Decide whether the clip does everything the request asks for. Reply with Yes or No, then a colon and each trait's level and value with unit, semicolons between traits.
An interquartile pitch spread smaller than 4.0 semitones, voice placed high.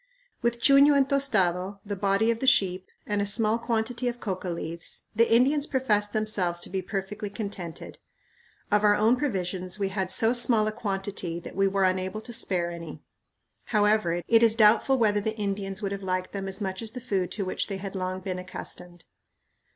Yes: average, 3.2 semitones; high, 205 Hz